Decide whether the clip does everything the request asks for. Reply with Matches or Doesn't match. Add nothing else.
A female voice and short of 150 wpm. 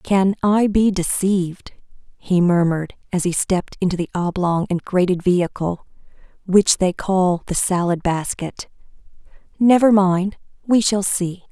Matches